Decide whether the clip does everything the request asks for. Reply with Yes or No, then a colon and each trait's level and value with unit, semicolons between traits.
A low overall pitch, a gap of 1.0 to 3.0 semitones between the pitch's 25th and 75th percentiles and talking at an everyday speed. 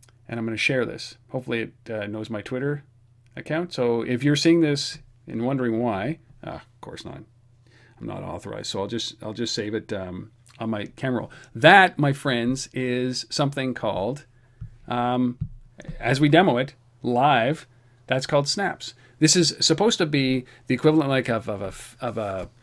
No: low, 125 Hz; average, 3.4 semitones; average, 180 wpm